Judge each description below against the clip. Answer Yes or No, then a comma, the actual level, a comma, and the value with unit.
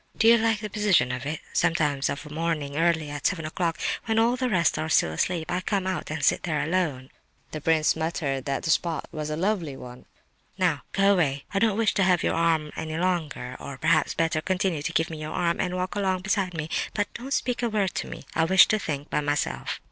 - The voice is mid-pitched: Yes, medium, 165 Hz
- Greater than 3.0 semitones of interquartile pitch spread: Yes, average, 3.9 semitones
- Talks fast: Yes, fast, 235 wpm